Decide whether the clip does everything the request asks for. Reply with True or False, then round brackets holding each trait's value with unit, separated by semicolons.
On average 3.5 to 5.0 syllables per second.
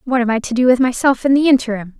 False (7.0 syllables/s)